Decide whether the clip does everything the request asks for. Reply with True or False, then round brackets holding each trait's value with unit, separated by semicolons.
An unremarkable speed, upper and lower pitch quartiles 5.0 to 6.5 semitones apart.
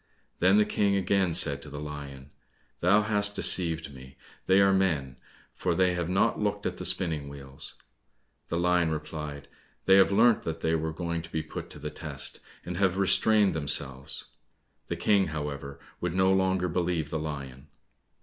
False (175 wpm; 4.5 semitones)